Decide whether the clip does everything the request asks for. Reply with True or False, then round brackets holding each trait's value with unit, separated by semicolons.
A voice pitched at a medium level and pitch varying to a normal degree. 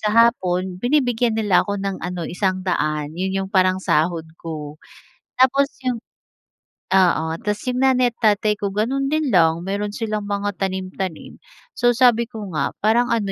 False (205 Hz; 4.3 semitones)